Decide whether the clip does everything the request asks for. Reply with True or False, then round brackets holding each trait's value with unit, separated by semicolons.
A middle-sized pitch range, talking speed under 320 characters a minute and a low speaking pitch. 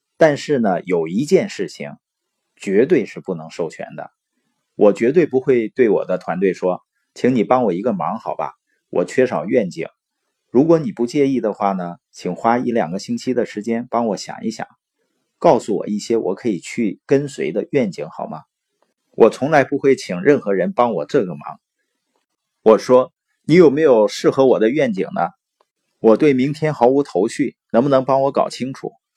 True (3.7 semitones; 255 characters per minute; 130 Hz)